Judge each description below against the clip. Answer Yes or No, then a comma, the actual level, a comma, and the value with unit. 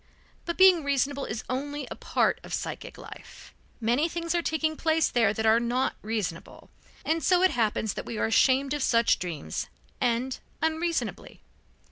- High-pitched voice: Yes, very high, 265 Hz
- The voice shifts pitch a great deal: Yes, wide, 5.8 semitones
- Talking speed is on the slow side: No, average, 165 wpm